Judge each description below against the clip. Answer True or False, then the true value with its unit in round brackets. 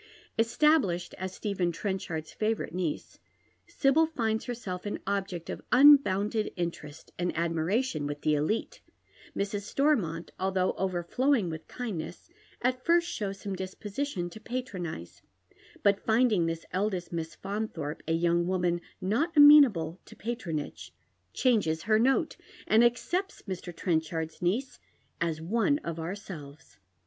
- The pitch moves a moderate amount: False (5.7 semitones)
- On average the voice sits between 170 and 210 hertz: True (190 Hz)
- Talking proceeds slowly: True (130 wpm)